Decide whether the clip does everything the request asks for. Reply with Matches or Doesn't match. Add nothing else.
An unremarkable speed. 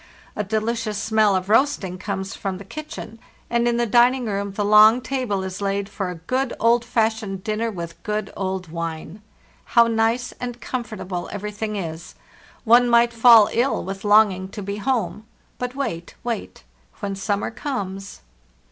Matches